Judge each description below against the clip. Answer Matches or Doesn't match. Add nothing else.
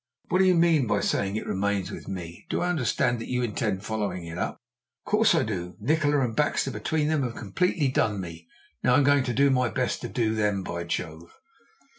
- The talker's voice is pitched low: Matches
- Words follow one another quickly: Matches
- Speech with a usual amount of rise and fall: Doesn't match